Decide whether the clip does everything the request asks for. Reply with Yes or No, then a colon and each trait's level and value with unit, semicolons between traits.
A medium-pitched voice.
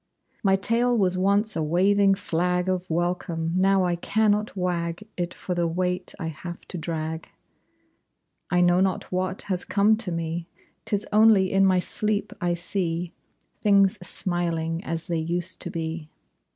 Yes: medium, 180 Hz